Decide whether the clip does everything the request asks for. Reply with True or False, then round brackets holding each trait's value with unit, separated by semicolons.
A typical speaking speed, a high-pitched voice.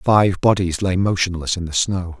False (190 wpm; 95 Hz)